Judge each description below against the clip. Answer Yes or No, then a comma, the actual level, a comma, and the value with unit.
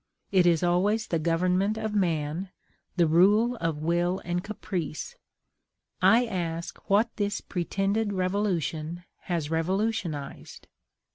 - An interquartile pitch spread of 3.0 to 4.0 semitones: Yes, average, 3.6 semitones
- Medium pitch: Yes, medium, 180 Hz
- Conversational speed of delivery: No, slow, 115 wpm